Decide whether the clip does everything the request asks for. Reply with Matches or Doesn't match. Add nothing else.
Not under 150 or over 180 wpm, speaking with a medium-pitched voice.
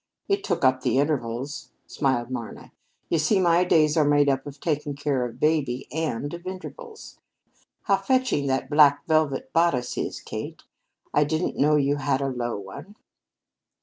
Matches